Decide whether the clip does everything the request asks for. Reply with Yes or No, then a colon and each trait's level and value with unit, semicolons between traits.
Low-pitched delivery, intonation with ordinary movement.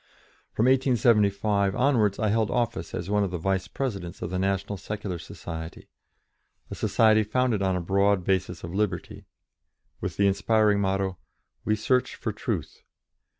No: low, 100 Hz; narrow, 2.3 semitones